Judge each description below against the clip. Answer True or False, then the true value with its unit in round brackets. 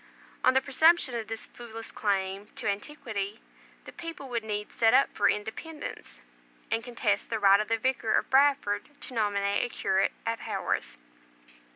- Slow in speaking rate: False (165 wpm)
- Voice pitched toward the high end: True (225 Hz)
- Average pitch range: True (4.0 semitones)